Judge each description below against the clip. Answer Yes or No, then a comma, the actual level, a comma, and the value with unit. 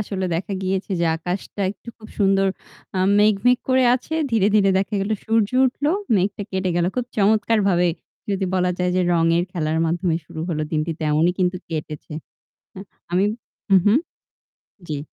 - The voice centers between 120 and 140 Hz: No, high, 190 Hz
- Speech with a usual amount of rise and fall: Yes, average, 3.4 semitones